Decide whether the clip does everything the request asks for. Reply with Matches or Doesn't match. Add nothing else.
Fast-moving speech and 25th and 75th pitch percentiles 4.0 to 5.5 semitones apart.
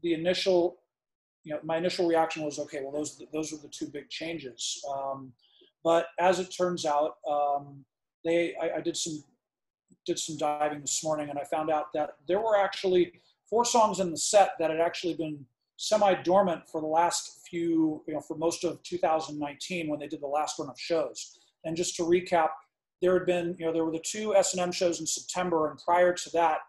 Doesn't match